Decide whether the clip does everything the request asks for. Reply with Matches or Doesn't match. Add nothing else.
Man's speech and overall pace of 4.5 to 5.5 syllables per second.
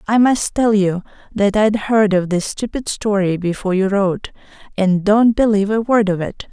Doesn't match